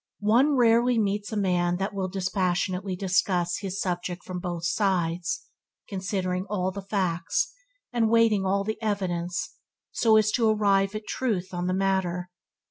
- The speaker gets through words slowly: No, average, 150 wpm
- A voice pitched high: Yes, high, 195 Hz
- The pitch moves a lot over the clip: No, average, 2.8 semitones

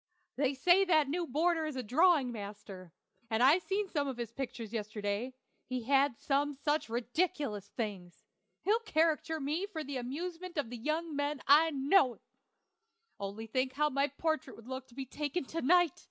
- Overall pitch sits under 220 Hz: No, very high, 280 Hz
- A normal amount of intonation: Yes, average, 5.0 semitones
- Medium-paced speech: Yes, average, 170 wpm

